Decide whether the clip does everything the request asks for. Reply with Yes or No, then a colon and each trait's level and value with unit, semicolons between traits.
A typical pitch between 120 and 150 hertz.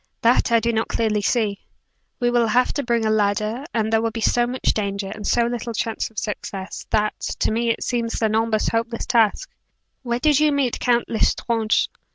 No: high, 230 Hz